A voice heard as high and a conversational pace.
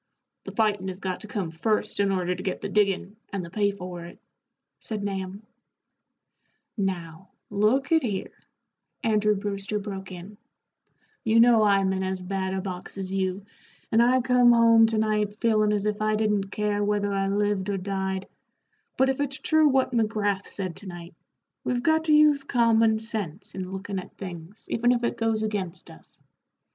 Yes: high, 205 Hz; average, 180 wpm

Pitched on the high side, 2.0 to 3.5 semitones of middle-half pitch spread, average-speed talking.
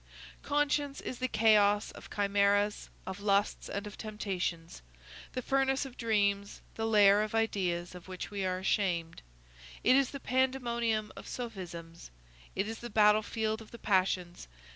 Yes: high, 210 Hz; average, 3.2 semitones; average, 150 wpm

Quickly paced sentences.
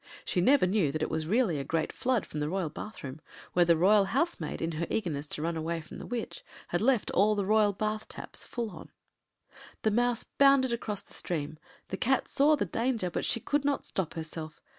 Yes: fast, 210 wpm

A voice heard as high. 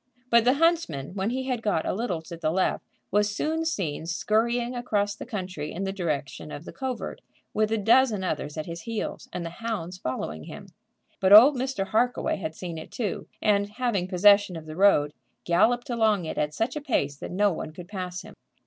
Yes: high, 200 Hz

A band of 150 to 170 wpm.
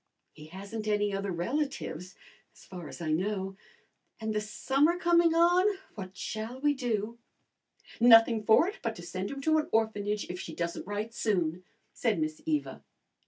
Yes: average, 165 wpm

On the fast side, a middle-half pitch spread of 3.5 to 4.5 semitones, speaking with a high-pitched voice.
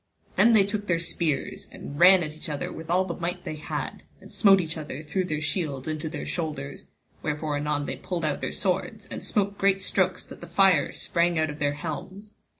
No: fast, 215 wpm; average, 3.9 semitones; medium, 165 Hz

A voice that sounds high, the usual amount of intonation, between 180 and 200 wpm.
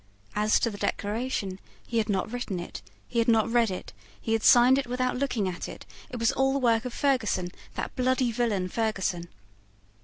Yes: high, 230 Hz; average, 3.6 semitones; average, 195 wpm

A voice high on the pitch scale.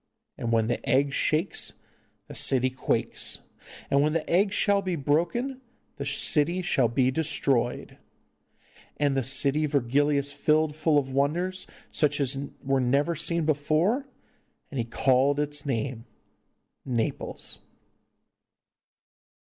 No: medium, 145 Hz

